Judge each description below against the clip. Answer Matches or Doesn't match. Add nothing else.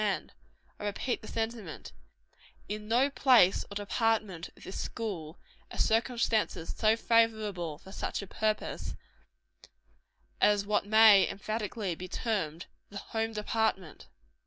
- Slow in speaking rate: Matches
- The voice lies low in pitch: Doesn't match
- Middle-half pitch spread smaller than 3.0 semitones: Matches